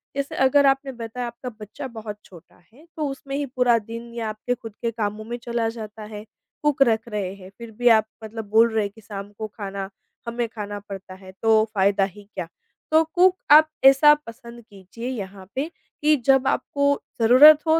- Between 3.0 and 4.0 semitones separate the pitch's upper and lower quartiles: No, average, 4.5 semitones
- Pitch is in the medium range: No, high, 230 Hz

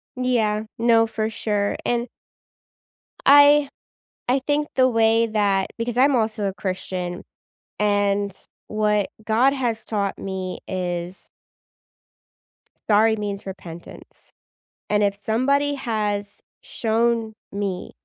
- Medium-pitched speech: No, high, 215 Hz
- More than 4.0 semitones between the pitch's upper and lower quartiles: No, average, 2.9 semitones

